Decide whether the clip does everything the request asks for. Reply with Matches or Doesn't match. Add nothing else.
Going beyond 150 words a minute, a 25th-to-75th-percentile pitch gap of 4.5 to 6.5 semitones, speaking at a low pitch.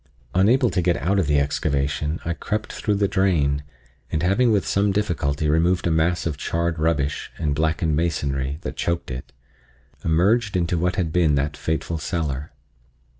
Doesn't match